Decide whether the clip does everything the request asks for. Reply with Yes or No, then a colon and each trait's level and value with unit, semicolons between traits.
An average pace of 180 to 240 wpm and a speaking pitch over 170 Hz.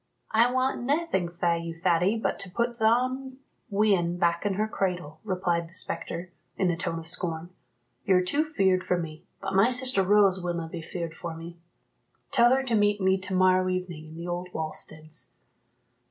Yes: average, 185 wpm; medium, 185 Hz